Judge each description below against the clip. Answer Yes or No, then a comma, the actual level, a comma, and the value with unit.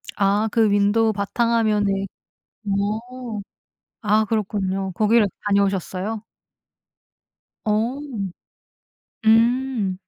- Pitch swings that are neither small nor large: No, narrow, 2.2 semitones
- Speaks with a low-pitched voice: No, high, 210 Hz